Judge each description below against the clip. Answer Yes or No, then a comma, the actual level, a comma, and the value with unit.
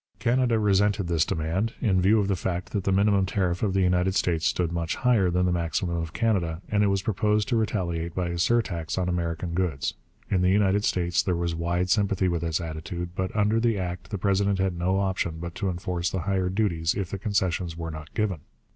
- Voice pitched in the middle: No, very low, 90 Hz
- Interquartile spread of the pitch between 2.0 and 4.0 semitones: Yes, average, 2.8 semitones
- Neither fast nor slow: No, fast, 220 wpm